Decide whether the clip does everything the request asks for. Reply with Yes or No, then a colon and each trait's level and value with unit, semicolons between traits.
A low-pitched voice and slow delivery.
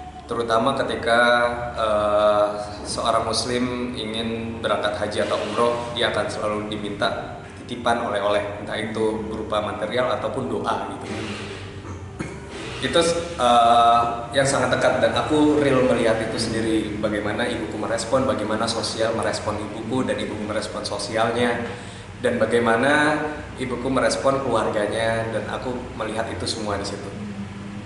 No: low, 110 Hz; average, 125 wpm